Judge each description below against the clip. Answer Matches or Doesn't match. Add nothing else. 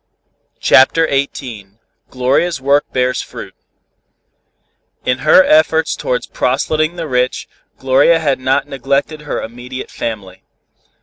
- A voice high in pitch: Doesn't match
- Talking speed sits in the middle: Doesn't match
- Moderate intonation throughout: Matches